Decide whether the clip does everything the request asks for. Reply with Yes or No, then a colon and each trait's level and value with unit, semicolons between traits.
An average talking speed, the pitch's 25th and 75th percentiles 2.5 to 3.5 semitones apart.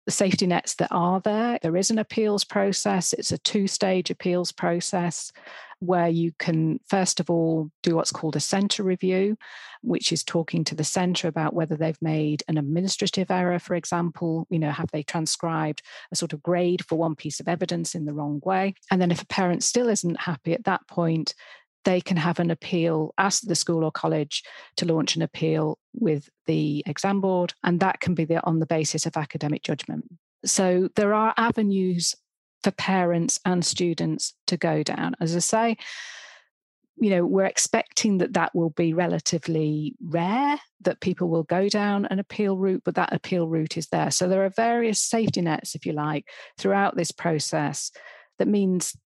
Yes: average, 190 wpm; average, 2.9 semitones